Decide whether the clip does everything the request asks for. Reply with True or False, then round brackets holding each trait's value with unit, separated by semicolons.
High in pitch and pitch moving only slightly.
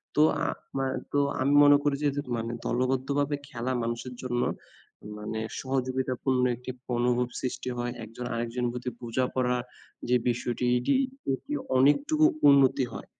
False (125 Hz; 1.8 semitones)